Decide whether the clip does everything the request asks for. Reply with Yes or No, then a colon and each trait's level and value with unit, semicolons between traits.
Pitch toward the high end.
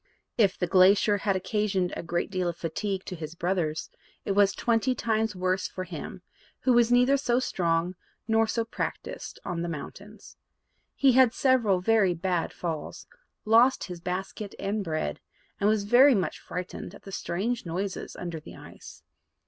Yes: high, 195 Hz